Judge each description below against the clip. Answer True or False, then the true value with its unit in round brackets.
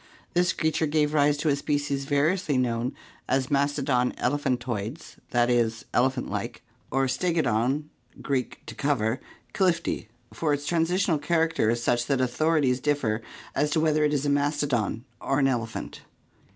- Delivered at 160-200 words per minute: False (150 wpm)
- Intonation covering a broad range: False (3.5 semitones)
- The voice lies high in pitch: False (140 Hz)